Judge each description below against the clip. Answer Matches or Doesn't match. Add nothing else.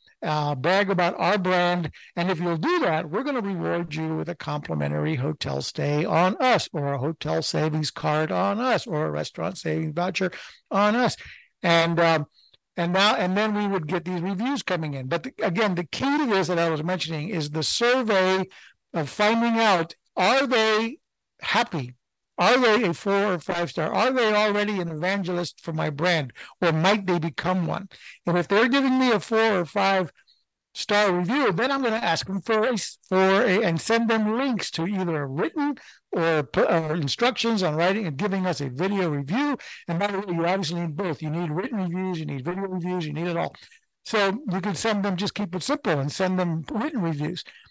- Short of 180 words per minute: Doesn't match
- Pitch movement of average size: Matches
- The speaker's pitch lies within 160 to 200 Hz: Matches